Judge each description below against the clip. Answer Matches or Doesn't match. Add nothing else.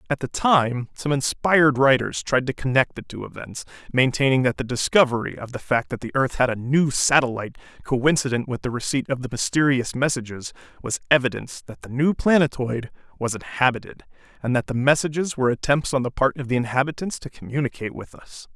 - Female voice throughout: Doesn't match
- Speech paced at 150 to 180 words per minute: Doesn't match